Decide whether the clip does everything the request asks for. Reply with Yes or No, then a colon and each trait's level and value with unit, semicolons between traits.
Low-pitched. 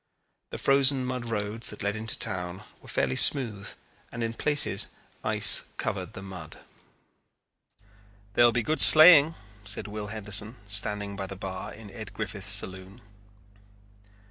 Yes: low, 105 Hz